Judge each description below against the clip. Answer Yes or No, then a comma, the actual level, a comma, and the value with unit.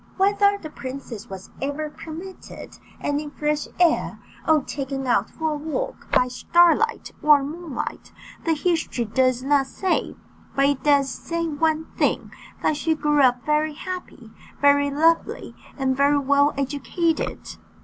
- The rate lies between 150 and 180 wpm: No, average, 140 wpm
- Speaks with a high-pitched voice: Yes, very high, 295 Hz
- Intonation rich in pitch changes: No, average, 2.8 semitones